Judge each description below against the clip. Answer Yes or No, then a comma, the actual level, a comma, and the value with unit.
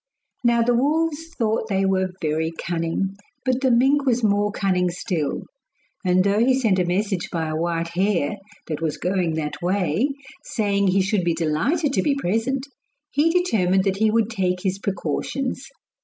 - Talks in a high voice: Yes, high, 195 Hz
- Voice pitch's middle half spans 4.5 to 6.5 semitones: Yes, average, 5.2 semitones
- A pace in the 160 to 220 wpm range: Yes, average, 170 wpm